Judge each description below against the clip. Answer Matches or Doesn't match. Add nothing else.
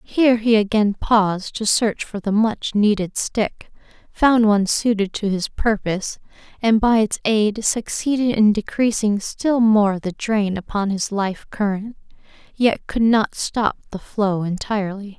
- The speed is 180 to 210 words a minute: Doesn't match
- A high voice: Matches